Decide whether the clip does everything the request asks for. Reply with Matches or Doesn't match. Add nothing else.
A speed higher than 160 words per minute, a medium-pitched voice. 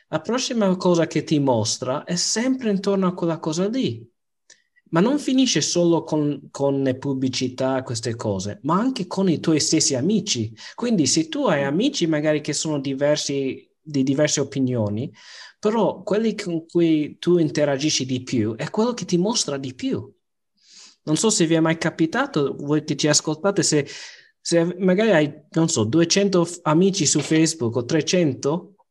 Matches